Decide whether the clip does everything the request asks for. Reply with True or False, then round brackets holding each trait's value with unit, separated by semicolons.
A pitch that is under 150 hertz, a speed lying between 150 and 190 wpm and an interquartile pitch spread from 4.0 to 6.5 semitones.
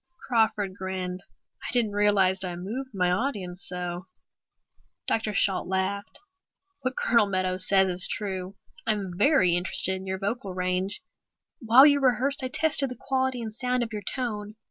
False (200 Hz; 155 wpm; 4.4 semitones)